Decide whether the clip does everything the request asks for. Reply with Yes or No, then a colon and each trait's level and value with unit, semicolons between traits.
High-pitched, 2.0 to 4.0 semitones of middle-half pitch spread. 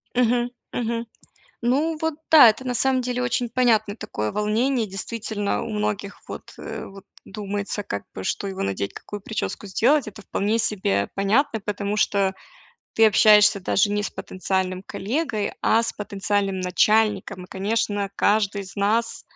Yes: high, 210 Hz; average, 2.7 semitones